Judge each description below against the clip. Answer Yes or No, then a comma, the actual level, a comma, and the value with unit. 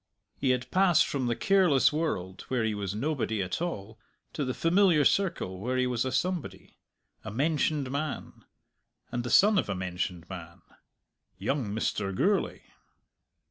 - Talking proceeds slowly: No, average, 155 wpm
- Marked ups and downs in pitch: Yes, wide, 7.5 semitones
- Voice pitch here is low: Yes, low, 130 Hz